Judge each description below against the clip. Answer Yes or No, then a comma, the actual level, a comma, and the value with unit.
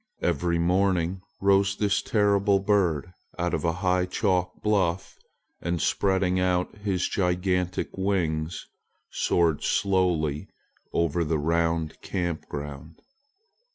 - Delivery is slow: Yes, slow, 115 wpm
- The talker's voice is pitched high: No, very low, 90 Hz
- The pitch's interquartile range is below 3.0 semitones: Yes, narrow, 2.5 semitones